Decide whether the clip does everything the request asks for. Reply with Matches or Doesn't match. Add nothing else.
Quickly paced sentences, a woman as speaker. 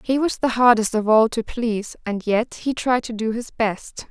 Matches